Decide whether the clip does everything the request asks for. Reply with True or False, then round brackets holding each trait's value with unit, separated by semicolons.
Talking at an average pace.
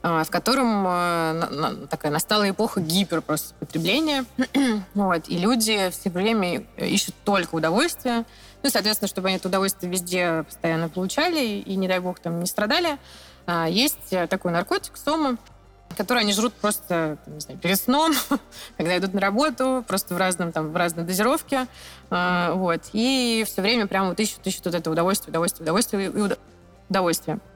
False (170 wpm)